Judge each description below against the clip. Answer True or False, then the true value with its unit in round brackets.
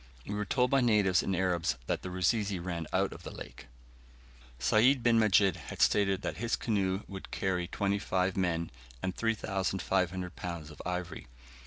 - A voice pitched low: True (95 Hz)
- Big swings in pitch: False (2.6 semitones)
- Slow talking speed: False (170 wpm)